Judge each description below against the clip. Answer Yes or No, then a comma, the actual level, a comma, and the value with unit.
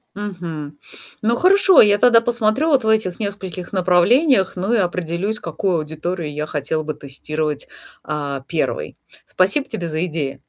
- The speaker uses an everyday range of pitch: No, wide, 5.9 semitones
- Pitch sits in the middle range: Yes, medium, 180 Hz